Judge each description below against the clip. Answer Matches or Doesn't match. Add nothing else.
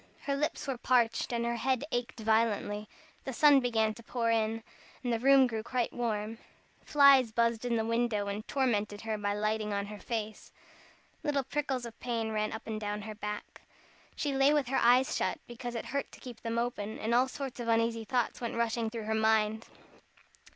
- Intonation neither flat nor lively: Doesn't match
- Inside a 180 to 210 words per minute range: Matches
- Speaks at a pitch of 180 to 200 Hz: Doesn't match